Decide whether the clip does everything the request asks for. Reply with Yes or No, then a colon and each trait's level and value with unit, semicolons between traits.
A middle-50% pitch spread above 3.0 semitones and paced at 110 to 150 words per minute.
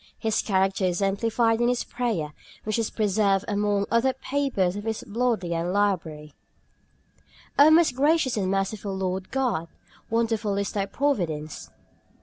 Yes: average, 3.7 semitones; average, 145 wpm